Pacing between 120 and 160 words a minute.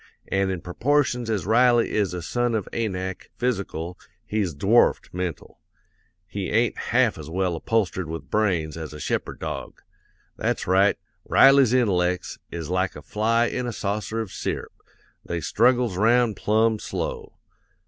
Yes: average, 150 wpm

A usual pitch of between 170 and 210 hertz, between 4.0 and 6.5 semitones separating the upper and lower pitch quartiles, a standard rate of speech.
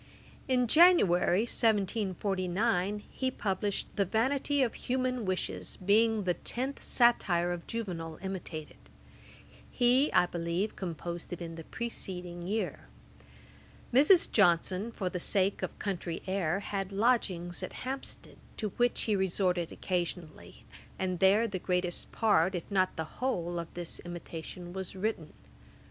No: high, 190 Hz; average, 4.4 semitones; slow, 130 wpm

